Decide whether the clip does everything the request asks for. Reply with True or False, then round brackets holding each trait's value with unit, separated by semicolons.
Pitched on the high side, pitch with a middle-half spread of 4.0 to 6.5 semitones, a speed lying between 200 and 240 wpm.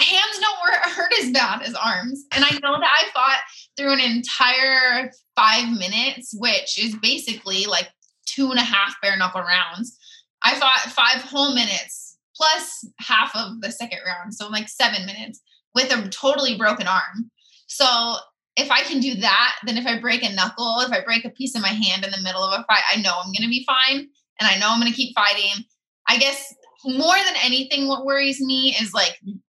True (240 Hz; 4.4 semitones; 205 wpm)